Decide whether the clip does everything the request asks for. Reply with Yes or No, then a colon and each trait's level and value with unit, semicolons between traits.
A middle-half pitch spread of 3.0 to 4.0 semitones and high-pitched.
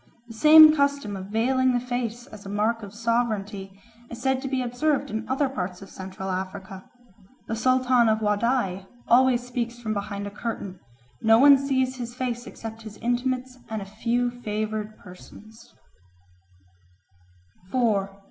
Yes: average, 3.5 semitones; high, 230 Hz